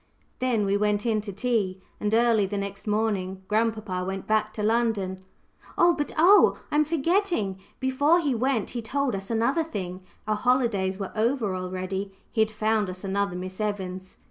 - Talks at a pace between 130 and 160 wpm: No, average, 170 wpm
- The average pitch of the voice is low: No, high, 215 Hz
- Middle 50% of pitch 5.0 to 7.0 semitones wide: No, average, 3.8 semitones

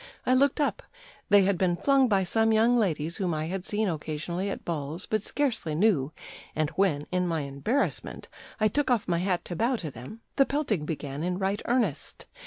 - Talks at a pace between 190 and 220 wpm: Yes, average, 195 wpm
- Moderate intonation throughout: No, wide, 5.9 semitones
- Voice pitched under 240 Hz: Yes, high, 190 Hz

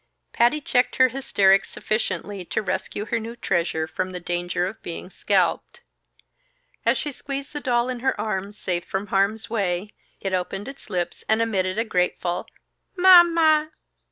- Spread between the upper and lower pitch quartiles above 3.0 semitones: Yes, average, 5.2 semitones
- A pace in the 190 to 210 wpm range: No, average, 160 wpm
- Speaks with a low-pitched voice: No, high, 210 Hz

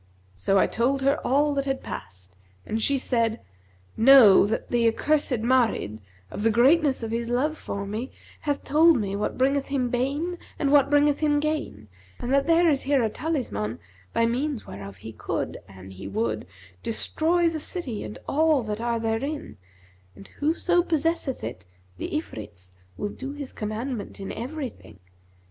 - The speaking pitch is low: No, very high, 255 Hz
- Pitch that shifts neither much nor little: No, wide, 5.8 semitones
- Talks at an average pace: Yes, average, 165 wpm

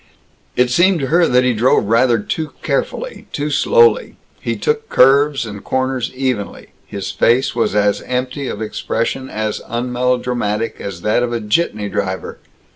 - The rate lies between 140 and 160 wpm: Yes, average, 155 wpm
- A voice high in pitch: No, low, 125 Hz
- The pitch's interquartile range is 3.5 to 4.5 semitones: Yes, average, 4.0 semitones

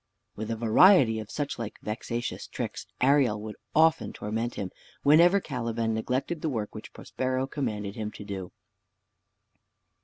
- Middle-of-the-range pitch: No, low, 115 Hz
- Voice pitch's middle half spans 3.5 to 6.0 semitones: Yes, average, 4.4 semitones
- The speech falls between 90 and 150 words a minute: Yes, average, 145 wpm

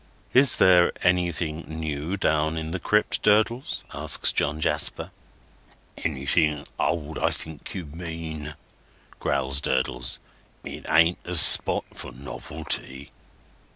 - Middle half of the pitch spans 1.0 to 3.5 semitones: Yes, average, 2.8 semitones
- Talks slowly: Yes, slow, 115 wpm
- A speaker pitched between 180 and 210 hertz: No, very low, 80 Hz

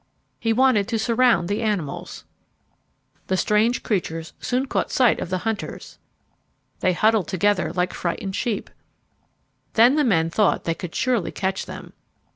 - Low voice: No, high, 210 Hz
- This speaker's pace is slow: No, average, 145 wpm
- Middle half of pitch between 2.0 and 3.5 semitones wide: No, average, 4.3 semitones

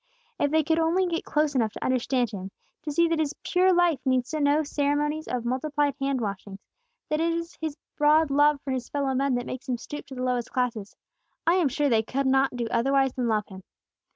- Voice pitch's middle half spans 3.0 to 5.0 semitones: Yes, average, 3.5 semitones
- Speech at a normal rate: No, fast, 220 wpm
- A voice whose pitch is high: Yes, very high, 275 Hz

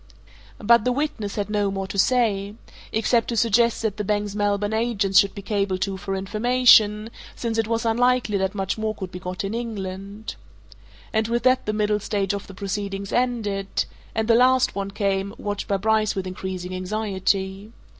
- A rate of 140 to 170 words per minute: No, average, 185 wpm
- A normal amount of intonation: No, narrow, 2.3 semitones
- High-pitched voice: Yes, high, 205 Hz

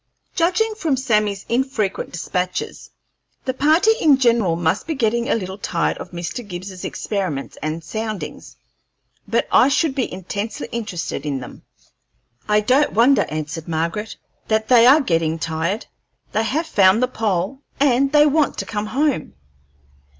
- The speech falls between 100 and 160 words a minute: Yes, average, 150 wpm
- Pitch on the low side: No, high, 215 Hz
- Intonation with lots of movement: Yes, wide, 6.9 semitones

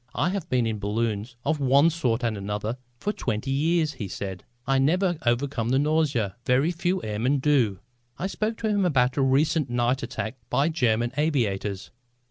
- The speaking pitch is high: No, low, 130 Hz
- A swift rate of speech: No, average, 175 wpm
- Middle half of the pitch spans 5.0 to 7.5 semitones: Yes, wide, 5.5 semitones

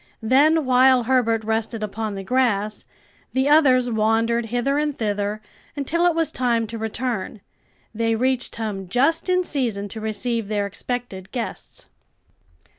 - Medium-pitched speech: No, high, 235 Hz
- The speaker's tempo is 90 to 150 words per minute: Yes, average, 140 wpm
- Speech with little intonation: No, average, 3.3 semitones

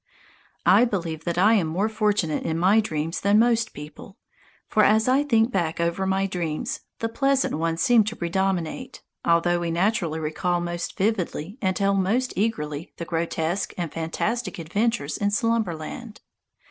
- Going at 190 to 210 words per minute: No, average, 160 wpm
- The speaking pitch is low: No, high, 190 Hz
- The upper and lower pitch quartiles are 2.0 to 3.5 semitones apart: No, average, 4.8 semitones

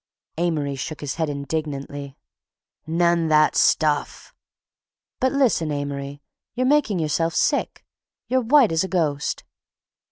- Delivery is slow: Yes, slow, 120 wpm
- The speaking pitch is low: No, medium, 160 Hz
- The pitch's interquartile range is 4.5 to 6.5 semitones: No, average, 3.7 semitones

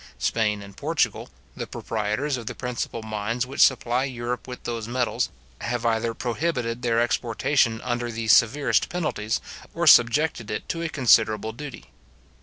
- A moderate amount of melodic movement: No, narrow, 2.3 semitones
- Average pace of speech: Yes, average, 150 wpm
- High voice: No, low, 120 Hz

